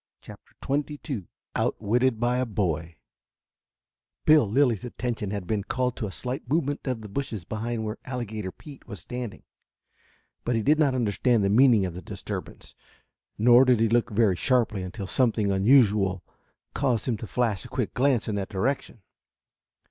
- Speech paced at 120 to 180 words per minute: Yes, average, 165 wpm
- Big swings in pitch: No, average, 3.9 semitones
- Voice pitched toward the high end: No, low, 115 Hz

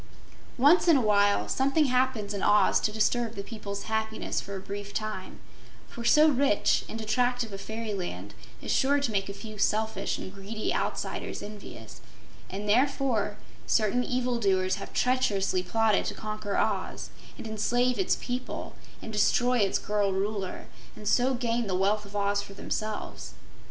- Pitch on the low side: No, high, 215 Hz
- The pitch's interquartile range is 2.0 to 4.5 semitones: Yes, average, 3.4 semitones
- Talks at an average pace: Yes, average, 160 wpm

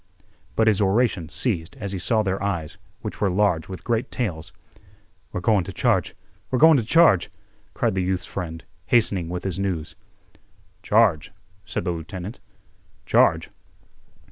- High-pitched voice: No, very low, 95 Hz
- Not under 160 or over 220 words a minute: No, average, 145 wpm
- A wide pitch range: No, average, 3.7 semitones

